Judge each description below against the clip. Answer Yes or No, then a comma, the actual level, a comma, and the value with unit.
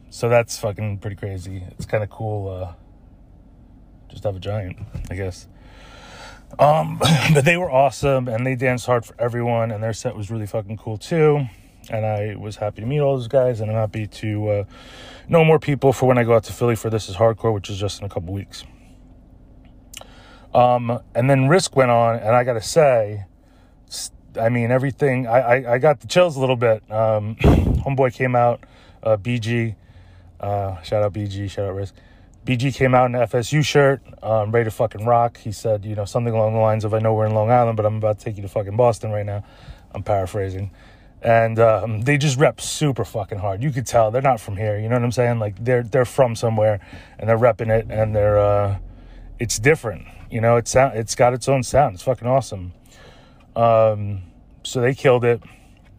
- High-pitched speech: No, low, 110 Hz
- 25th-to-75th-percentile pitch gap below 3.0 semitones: No, average, 3.3 semitones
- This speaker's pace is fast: Yes, fast, 210 wpm